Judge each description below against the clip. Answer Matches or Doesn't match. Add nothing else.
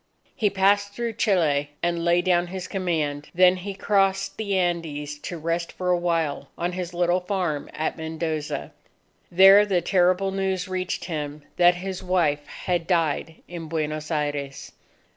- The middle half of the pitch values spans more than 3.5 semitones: Doesn't match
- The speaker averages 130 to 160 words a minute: Matches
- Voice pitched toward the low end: Doesn't match